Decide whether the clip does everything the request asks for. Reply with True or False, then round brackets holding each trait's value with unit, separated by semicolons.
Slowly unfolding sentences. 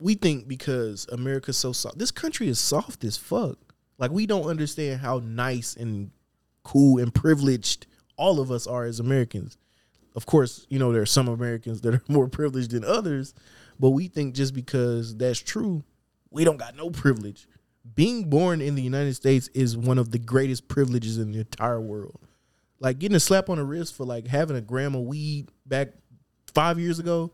False (195 wpm)